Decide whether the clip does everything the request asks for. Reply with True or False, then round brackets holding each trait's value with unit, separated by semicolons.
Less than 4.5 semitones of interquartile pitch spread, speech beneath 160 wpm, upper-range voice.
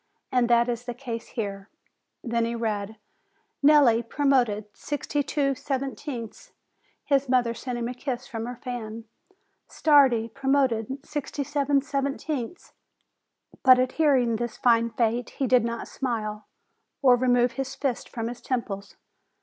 True (2.9 semitones; 145 wpm; 245 Hz)